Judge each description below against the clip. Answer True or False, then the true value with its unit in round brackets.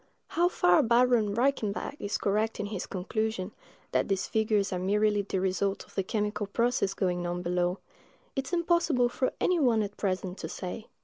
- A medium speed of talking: True (180 wpm)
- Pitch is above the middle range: True (210 Hz)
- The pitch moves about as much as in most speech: True (3.8 semitones)